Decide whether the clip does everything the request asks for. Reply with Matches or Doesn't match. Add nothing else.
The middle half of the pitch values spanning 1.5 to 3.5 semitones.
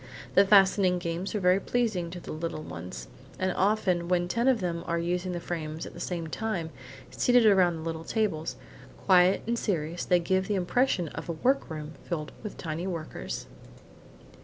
Matches